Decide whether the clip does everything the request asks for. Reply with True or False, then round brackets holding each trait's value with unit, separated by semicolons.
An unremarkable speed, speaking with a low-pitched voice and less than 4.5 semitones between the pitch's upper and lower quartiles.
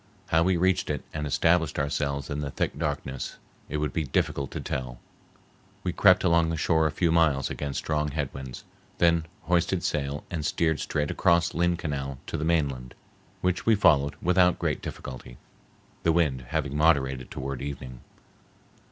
True (170 wpm; 75 Hz; 3.4 semitones)